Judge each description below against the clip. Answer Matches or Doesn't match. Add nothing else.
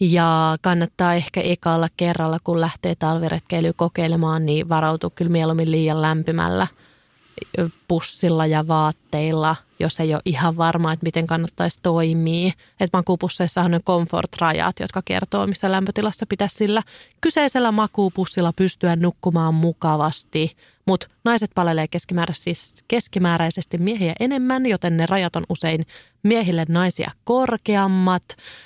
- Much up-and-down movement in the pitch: Doesn't match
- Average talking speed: Matches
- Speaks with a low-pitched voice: Doesn't match